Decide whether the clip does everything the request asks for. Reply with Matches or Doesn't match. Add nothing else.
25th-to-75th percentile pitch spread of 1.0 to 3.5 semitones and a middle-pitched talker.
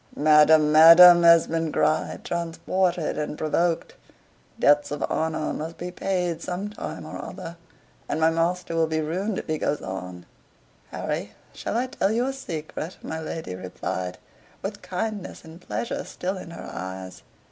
Matches